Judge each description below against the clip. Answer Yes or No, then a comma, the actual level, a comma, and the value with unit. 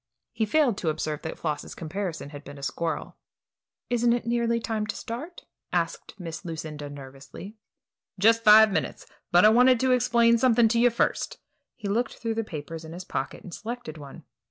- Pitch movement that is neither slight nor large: No, wide, 6.8 semitones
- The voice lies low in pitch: No, high, 210 Hz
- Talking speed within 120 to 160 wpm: No, average, 180 wpm